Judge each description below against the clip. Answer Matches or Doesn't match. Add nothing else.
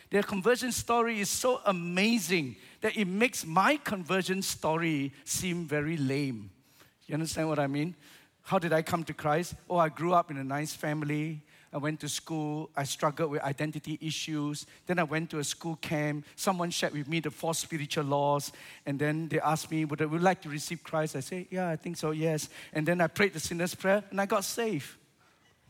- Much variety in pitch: Doesn't match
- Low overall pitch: Doesn't match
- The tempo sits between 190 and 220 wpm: Matches